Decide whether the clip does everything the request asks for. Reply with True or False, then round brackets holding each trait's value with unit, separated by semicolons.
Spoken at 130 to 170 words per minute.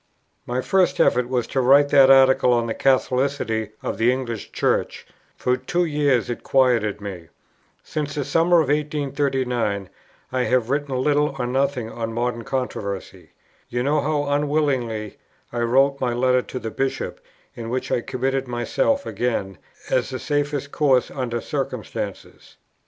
True (150 wpm)